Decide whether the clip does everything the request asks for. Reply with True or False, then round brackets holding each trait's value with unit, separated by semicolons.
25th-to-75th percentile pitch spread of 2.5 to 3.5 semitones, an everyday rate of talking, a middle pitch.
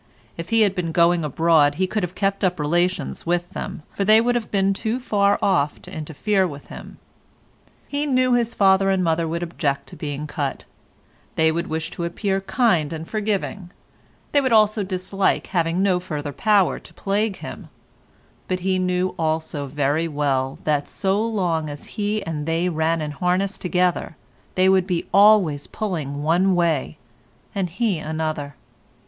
False (3.9 semitones; 170 wpm; 180 Hz)